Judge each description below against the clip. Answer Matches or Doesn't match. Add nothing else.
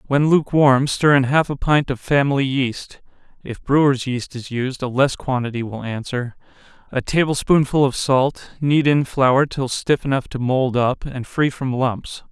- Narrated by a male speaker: Matches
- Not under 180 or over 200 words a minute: Matches